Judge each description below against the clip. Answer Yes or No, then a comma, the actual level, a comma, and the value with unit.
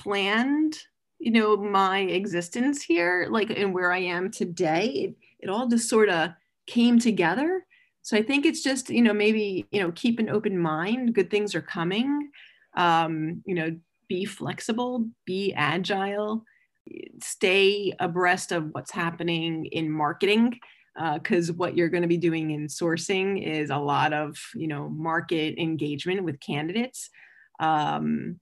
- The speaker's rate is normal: Yes, average, 155 wpm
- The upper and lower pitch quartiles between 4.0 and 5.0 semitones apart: No, wide, 5.4 semitones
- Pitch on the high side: Yes, high, 195 Hz